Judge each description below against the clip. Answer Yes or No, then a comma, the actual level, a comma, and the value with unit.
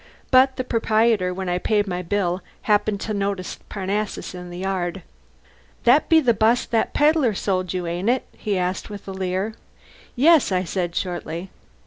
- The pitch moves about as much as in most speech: Yes, average, 3.6 semitones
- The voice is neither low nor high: No, high, 195 Hz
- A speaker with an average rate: Yes, average, 165 wpm